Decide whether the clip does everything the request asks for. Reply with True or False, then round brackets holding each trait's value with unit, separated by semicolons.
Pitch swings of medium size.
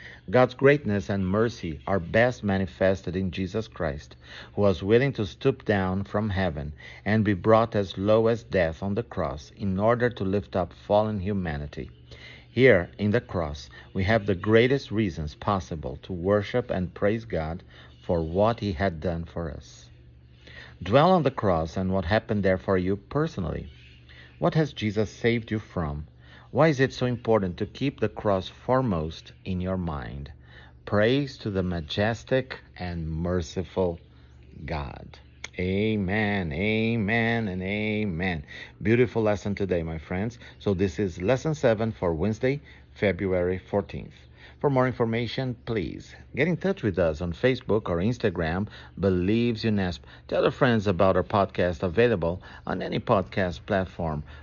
True (5.0 semitones)